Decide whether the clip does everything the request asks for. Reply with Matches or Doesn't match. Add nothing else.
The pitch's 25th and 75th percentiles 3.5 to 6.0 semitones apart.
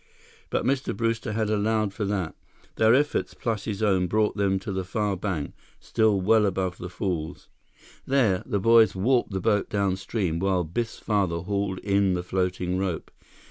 Doesn't match